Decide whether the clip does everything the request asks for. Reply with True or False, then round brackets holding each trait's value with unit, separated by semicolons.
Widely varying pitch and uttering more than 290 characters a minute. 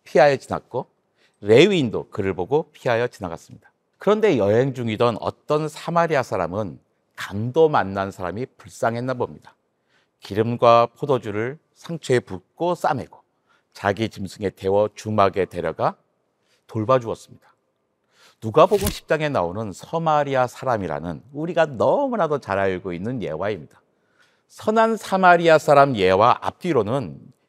True (7.9 semitones; 305 characters per minute)